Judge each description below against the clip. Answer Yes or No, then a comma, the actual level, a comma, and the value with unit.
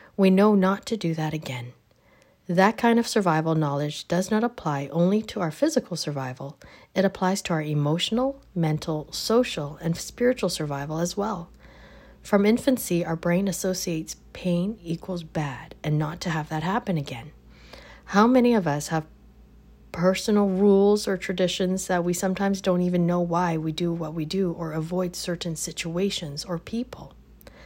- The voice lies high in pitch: No, medium, 175 Hz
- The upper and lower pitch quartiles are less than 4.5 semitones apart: Yes, average, 3.8 semitones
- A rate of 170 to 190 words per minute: No, average, 160 wpm